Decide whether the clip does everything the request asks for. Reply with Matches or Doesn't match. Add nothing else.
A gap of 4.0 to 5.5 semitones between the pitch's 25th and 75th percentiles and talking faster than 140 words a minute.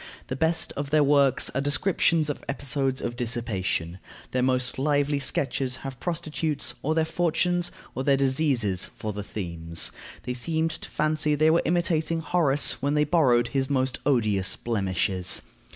Matches